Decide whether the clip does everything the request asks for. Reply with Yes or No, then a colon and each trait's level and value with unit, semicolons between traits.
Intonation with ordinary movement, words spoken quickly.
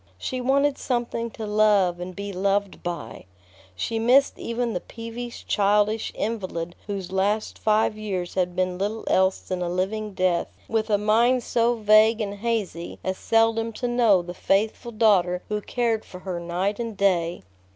No: average, 3.5 semitones; average, 165 wpm